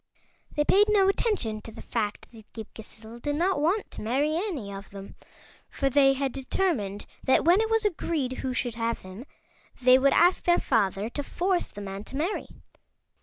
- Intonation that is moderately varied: No, wide, 7.9 semitones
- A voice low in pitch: No, very high, 270 Hz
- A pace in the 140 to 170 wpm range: No, average, 190 wpm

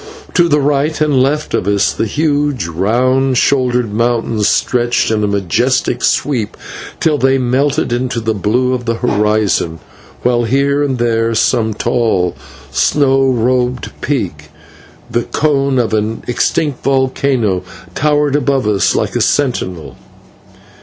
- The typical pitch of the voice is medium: No, low, 125 Hz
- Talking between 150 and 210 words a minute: No, slow, 135 wpm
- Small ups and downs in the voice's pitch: No, average, 3.9 semitones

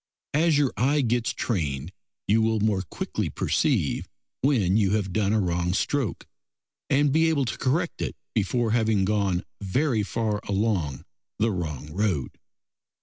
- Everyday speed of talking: Yes, average, 145 wpm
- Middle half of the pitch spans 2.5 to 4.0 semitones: No, average, 4.7 semitones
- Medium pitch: No, low, 110 Hz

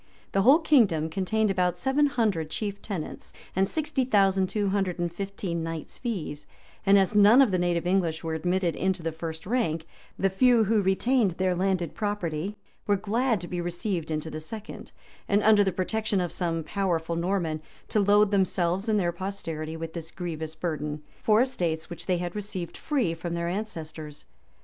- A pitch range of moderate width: Yes, average, 3.9 semitones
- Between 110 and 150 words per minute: No, average, 180 wpm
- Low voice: No, medium, 185 Hz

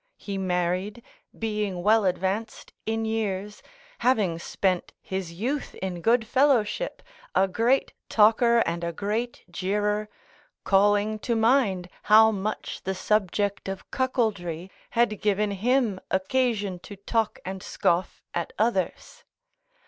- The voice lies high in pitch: Yes, high, 210 Hz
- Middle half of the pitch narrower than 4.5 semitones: Yes, average, 3.1 semitones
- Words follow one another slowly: Yes, slow, 120 wpm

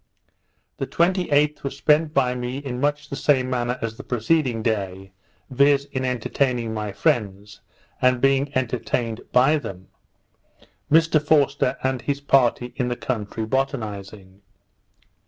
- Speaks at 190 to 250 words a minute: No, slow, 135 wpm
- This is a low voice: Yes, low, 130 Hz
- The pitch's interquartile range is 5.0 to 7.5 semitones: No, average, 3.9 semitones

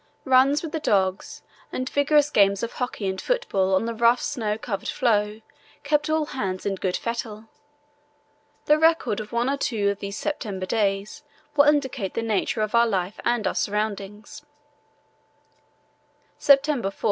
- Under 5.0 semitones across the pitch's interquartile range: No, wide, 5.6 semitones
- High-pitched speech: Yes, high, 225 Hz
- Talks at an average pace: Yes, average, 160 wpm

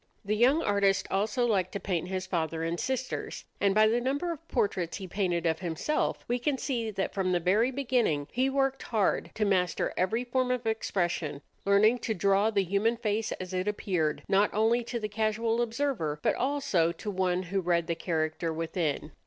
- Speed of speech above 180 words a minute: Yes, average, 195 wpm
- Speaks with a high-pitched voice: Yes, high, 200 Hz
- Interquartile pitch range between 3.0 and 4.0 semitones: No, average, 5.0 semitones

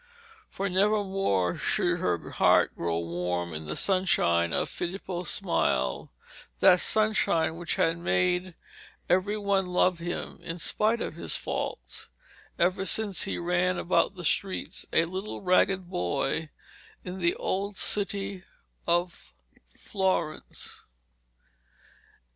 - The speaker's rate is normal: No, slow, 120 wpm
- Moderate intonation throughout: Yes, average, 3.0 semitones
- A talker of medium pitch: Yes, medium, 180 Hz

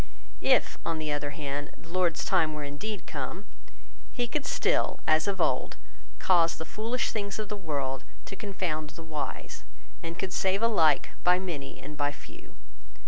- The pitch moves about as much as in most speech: Yes, average, 4.7 semitones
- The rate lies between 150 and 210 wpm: Yes, average, 170 wpm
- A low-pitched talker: No, medium, 165 Hz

